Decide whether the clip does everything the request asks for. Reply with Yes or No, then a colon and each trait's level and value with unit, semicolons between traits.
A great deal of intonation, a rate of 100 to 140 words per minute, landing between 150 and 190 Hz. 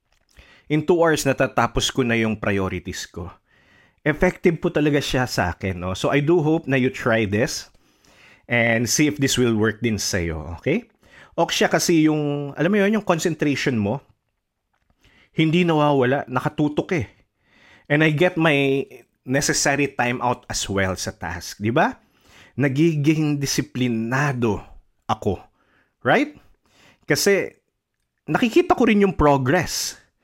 No: wide, 5.9 semitones; slow, 135 wpm; low, 135 Hz